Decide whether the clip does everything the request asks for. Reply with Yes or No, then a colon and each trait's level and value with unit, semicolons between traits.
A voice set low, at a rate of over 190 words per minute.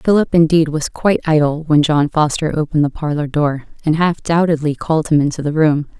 No: medium, 155 Hz; average, 200 wpm